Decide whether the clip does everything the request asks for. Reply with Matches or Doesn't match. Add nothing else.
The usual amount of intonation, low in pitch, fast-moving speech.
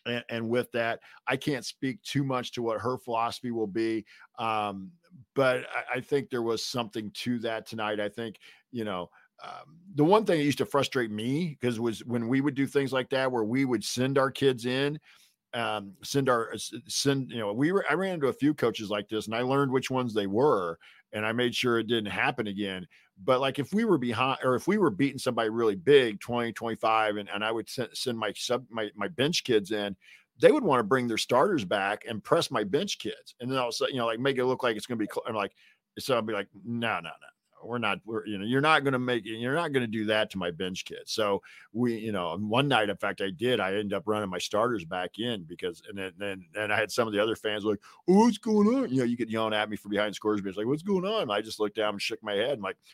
Matches